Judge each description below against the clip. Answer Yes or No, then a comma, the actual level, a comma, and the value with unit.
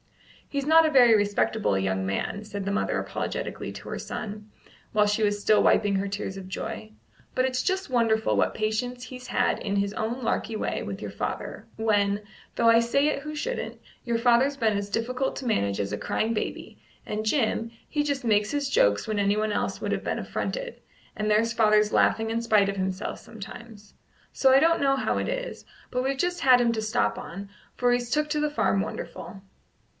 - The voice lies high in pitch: Yes, high, 225 Hz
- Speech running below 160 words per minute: No, fast, 205 wpm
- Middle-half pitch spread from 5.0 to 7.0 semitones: No, average, 4.0 semitones